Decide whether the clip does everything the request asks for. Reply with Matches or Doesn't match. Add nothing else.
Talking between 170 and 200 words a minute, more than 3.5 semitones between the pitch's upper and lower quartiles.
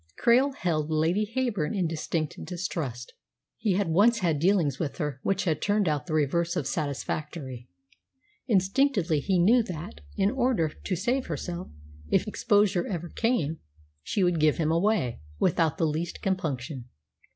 Doesn't match